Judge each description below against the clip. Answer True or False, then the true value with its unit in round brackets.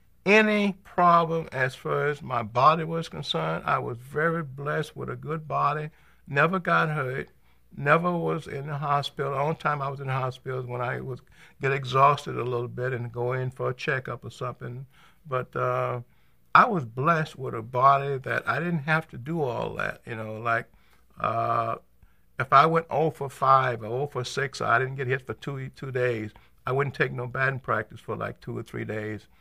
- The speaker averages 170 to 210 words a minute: True (205 wpm)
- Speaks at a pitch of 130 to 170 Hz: True (135 Hz)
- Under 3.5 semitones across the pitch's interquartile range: False (3.8 semitones)